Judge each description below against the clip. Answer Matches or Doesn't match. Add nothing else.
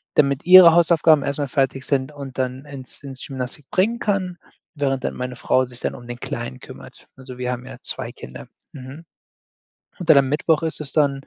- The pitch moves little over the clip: Doesn't match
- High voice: Doesn't match